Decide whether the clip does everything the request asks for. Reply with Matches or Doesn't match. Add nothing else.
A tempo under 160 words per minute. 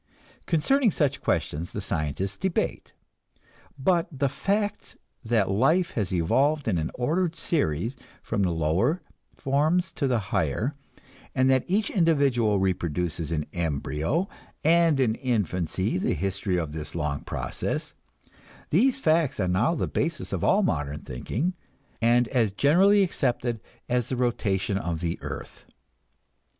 Matches